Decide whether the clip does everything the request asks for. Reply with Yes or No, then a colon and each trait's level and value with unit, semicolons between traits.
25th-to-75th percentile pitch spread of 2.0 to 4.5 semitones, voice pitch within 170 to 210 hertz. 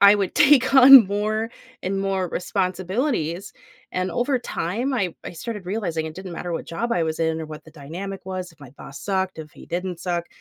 Yes: average, 3.8 semitones; medium, 185 Hz